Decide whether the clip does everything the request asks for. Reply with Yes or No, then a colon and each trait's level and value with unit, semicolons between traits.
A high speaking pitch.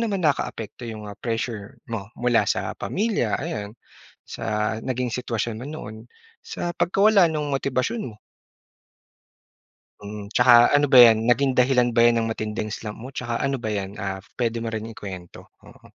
No: low, 120 Hz